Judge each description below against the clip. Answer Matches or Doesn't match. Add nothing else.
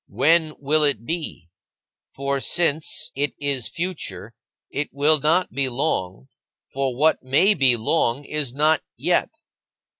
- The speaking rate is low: Matches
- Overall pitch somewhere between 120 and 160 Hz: Matches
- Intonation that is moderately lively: Matches